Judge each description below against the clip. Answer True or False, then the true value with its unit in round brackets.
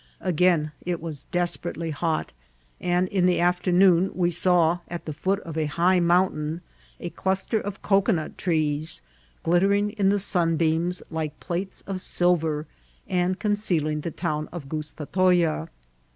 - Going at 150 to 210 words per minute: False (140 wpm)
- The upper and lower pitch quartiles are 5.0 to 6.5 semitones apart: False (2.6 semitones)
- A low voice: False (175 Hz)